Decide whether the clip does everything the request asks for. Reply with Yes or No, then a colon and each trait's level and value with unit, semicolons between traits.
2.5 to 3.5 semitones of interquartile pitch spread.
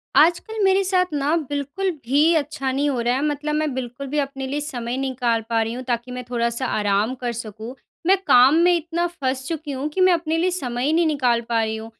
No: average, 4.4 semitones